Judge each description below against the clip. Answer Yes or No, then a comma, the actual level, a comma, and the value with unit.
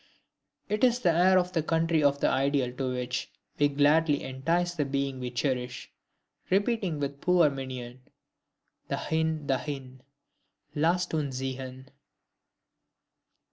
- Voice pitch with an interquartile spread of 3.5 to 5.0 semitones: Yes, average, 4.0 semitones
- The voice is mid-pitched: Yes, medium, 145 Hz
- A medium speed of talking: No, slow, 125 wpm